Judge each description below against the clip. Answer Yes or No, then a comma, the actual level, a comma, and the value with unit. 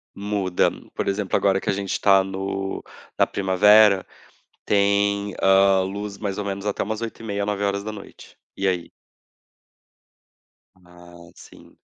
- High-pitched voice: No, low, 100 Hz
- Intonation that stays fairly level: Yes, narrow, 1.0 semitones